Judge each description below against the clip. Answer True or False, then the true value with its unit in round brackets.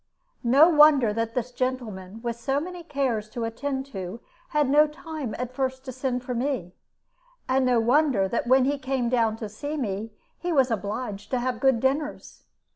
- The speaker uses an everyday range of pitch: True (3.5 semitones)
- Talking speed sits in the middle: True (185 wpm)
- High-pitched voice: True (255 Hz)